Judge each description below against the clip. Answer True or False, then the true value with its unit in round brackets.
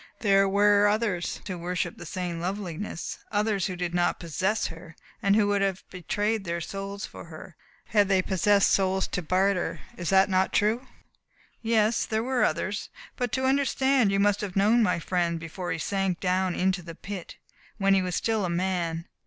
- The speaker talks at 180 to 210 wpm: True (185 wpm)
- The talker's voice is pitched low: False (195 Hz)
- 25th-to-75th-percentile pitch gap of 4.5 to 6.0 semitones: False (2.7 semitones)